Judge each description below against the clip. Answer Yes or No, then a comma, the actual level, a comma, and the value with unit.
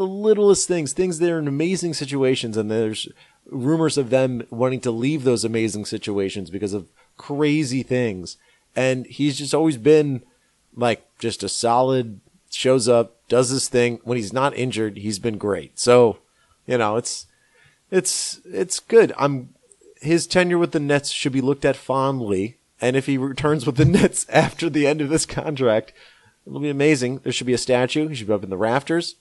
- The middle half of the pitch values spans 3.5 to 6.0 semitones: Yes, average, 4.5 semitones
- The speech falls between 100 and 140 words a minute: No, average, 185 wpm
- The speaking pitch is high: No, low, 135 Hz